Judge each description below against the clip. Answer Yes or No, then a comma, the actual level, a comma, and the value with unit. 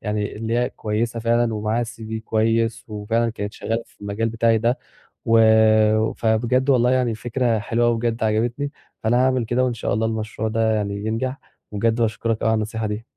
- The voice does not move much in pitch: Yes, narrow, 1.4 semitones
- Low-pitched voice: Yes, low, 115 Hz